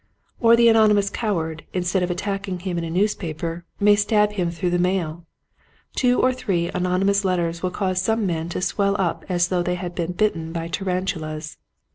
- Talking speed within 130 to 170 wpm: No, average, 190 wpm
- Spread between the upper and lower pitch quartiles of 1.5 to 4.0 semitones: Yes, average, 2.9 semitones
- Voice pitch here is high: No, medium, 180 Hz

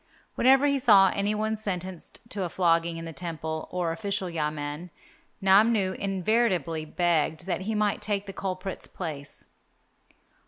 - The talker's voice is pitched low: No, medium, 185 Hz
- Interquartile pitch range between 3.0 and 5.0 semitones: Yes, average, 3.6 semitones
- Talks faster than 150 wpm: No, average, 145 wpm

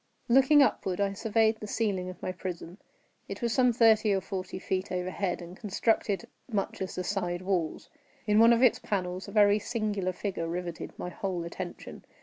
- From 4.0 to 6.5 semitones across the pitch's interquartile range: No, average, 3.2 semitones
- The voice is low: No, high, 195 Hz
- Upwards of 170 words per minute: Yes, average, 180 wpm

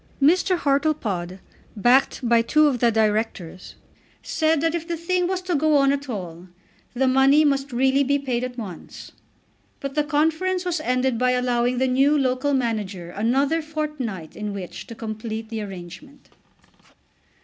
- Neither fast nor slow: Yes, average, 160 wpm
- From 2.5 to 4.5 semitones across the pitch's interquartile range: No, average, 5.1 semitones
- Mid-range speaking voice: No, very high, 260 Hz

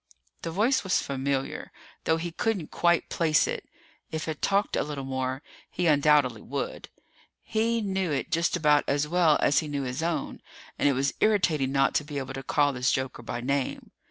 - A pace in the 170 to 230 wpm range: Yes, average, 190 wpm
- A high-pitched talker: No, medium, 150 Hz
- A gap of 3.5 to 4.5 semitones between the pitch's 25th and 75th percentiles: Yes, average, 4.1 semitones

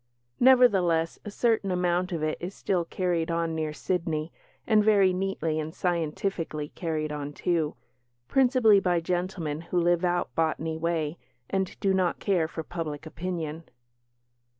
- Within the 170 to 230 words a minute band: No, average, 145 wpm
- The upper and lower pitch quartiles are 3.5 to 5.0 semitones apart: No, average, 2.9 semitones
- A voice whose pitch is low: No, medium, 175 Hz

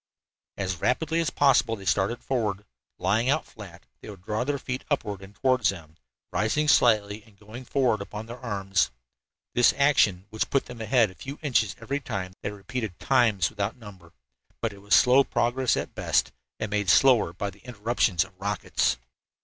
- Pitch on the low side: Yes, low, 110 Hz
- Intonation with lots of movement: No, average, 4.2 semitones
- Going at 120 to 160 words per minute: No, average, 180 wpm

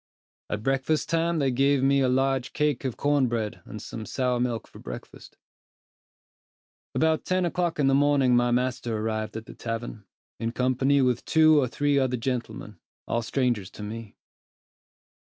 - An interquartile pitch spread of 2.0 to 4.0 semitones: Yes, average, 3.6 semitones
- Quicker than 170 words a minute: No, average, 165 wpm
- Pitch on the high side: No, low, 130 Hz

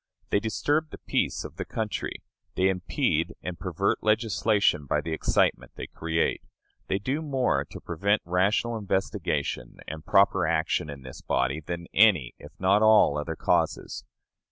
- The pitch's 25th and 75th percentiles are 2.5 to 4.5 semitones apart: No, average, 5.1 semitones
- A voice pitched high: No, very low, 95 Hz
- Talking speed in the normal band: Yes, average, 155 wpm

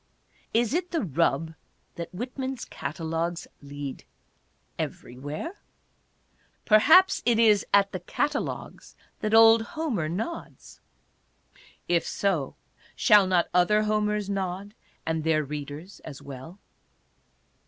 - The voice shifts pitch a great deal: Yes, wide, 5.8 semitones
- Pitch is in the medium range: No, high, 195 Hz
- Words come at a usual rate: No, slow, 110 wpm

